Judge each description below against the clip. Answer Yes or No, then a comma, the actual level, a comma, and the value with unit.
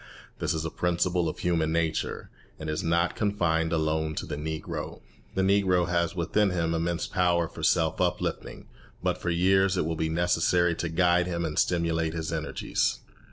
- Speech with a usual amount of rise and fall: No, narrow, 1.5 semitones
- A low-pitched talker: Yes, very low, 85 Hz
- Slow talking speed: No, average, 175 wpm